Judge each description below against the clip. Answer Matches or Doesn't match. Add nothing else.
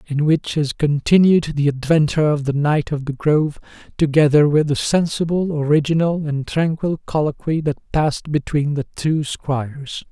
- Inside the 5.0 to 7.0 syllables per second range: Doesn't match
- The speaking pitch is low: Doesn't match